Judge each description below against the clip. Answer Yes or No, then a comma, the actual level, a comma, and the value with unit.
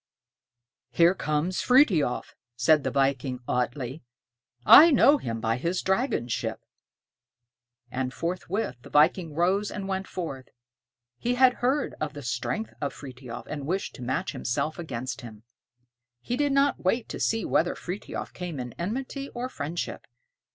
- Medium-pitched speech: Yes, medium, 165 Hz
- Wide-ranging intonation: Yes, wide, 8.3 semitones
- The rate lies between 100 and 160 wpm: Yes, average, 145 wpm